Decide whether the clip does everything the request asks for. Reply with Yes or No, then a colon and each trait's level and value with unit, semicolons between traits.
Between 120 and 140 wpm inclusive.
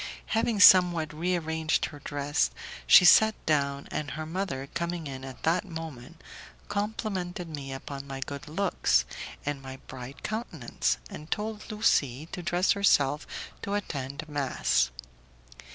Yes: slow, 135 wpm